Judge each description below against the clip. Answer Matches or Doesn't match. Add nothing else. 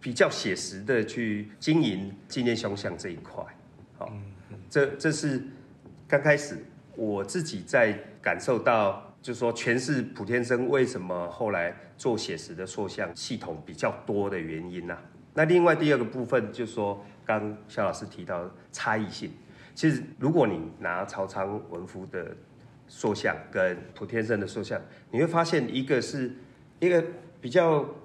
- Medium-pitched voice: Doesn't match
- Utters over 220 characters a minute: Matches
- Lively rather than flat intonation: Matches